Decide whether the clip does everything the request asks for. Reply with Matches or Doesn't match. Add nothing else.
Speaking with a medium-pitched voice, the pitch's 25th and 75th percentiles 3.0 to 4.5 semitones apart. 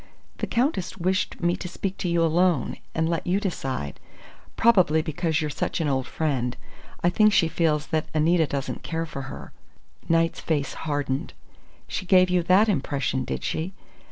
Matches